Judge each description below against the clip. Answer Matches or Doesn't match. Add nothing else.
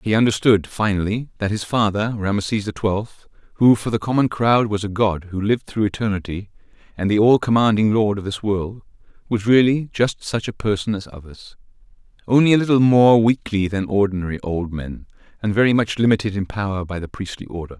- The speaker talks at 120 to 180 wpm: Doesn't match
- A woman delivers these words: Doesn't match